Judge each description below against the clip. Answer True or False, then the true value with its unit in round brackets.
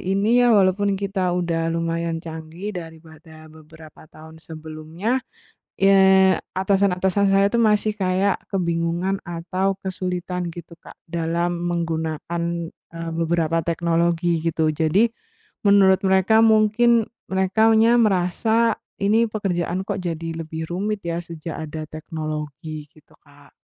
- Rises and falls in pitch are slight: False (3.3 semitones)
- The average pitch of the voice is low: False (175 Hz)